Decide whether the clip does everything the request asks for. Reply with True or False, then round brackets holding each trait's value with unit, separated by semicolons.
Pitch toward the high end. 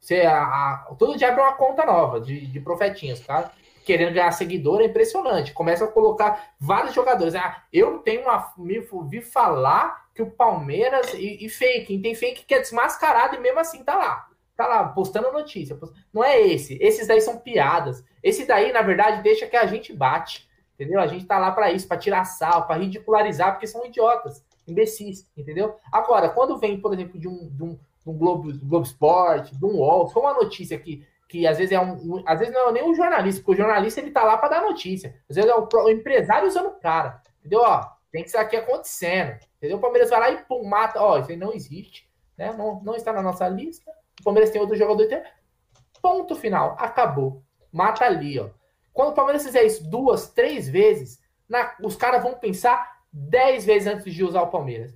True (210 Hz)